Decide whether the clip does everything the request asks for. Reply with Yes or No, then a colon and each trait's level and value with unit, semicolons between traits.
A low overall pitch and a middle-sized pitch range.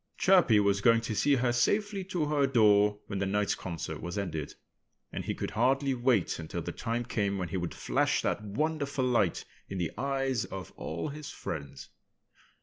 No: low, 115 Hz; wide, 5.8 semitones